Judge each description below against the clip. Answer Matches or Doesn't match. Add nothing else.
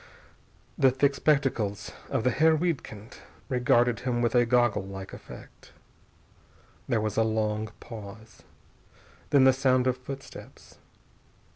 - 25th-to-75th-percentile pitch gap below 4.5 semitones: Matches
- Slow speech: Matches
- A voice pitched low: Matches